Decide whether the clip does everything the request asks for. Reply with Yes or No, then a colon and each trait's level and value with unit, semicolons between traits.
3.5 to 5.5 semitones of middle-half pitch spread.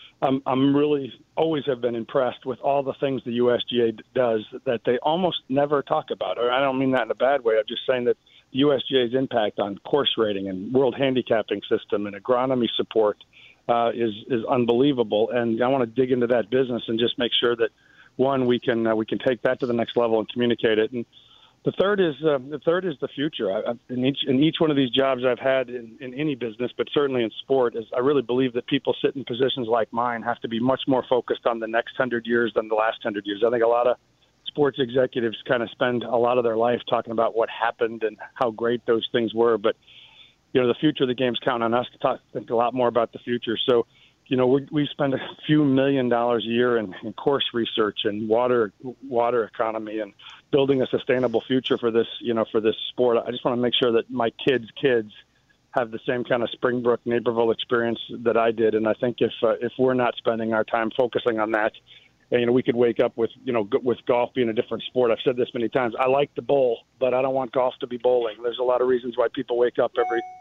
No: narrow, 2.4 semitones